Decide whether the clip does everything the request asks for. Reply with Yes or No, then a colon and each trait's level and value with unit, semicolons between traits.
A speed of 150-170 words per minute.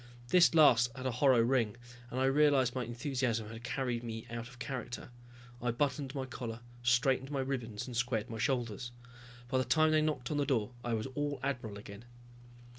No: average, 190 wpm